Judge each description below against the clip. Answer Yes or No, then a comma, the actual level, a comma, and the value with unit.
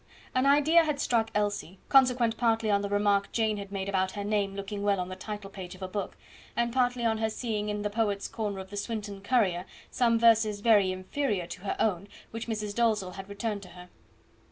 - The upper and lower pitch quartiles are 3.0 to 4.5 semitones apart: No, narrow, 2.5 semitones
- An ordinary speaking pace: No, fast, 215 wpm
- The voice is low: No, high, 210 Hz